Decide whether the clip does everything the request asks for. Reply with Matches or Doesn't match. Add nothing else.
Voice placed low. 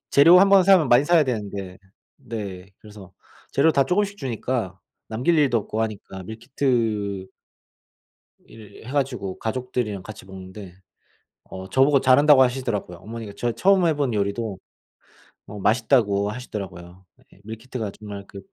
Matches